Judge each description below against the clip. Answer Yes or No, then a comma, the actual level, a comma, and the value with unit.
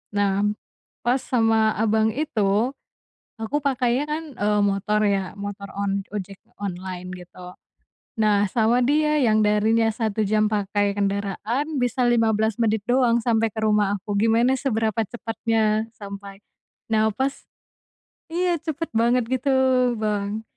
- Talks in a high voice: Yes, high, 220 Hz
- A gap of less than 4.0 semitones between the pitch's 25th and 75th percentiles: Yes, average, 2.9 semitones